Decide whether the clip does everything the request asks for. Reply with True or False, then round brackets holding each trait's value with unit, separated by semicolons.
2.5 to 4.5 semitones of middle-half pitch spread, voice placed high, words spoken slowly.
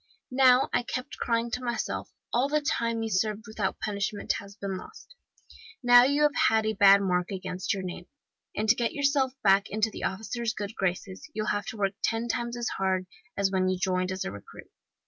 False (3.7 semitones; 215 Hz; 205 wpm)